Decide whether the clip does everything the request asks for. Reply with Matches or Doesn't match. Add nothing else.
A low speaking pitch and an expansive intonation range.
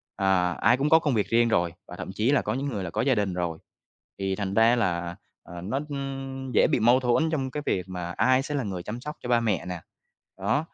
Matches